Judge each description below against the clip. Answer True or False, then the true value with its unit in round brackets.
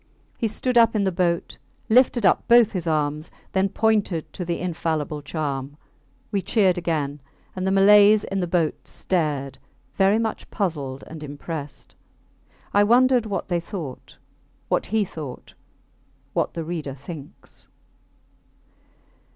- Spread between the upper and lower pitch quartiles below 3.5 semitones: False (5.2 semitones)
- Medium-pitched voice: True (175 Hz)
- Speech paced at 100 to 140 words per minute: True (135 wpm)